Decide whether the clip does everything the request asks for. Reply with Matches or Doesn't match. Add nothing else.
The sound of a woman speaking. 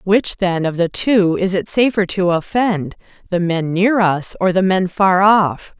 Matches